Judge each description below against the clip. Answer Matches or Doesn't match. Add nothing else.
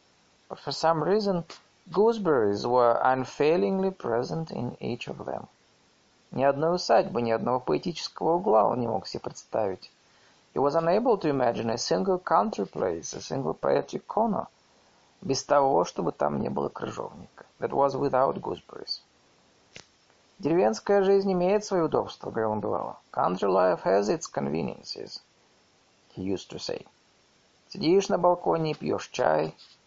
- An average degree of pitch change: Doesn't match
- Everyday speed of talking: Matches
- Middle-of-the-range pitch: Matches